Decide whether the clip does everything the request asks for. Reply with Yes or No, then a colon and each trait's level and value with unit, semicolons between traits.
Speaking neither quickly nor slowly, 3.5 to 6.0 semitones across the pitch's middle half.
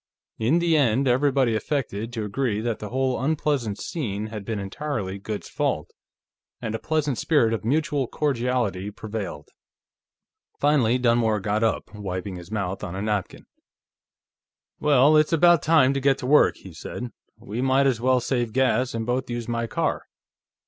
Yes: average, 160 wpm; average, 4.4 semitones